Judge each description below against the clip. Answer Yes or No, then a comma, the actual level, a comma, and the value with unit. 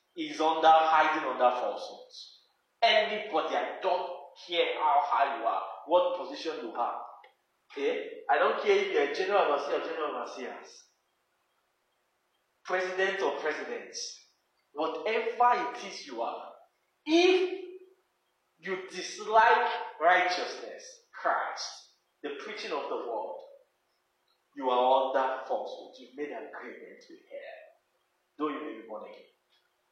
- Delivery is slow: Yes, slow, 125 wpm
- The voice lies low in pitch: No, high, 230 Hz